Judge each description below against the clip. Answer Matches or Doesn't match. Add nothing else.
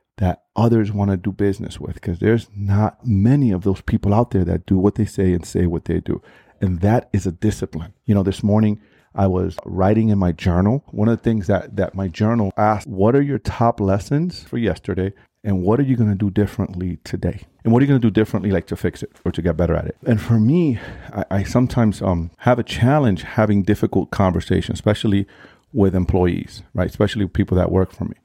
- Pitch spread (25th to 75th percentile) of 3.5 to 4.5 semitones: Doesn't match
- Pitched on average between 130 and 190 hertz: Doesn't match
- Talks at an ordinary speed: Doesn't match